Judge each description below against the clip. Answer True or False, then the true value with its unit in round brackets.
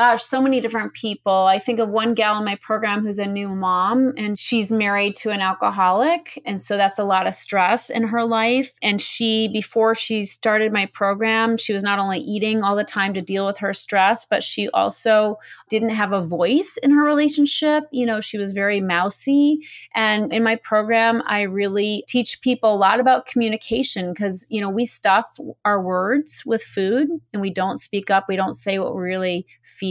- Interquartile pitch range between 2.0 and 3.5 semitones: True (2.8 semitones)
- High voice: True (215 Hz)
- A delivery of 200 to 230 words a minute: True (205 wpm)